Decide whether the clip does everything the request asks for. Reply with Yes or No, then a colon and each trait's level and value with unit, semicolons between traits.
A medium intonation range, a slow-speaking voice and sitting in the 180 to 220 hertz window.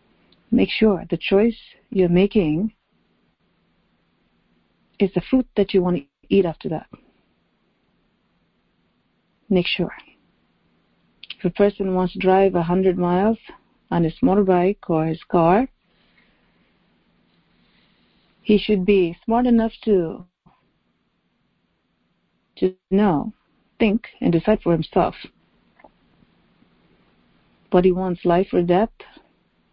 Yes: average, 3.3 semitones; slow, 105 wpm; medium, 185 Hz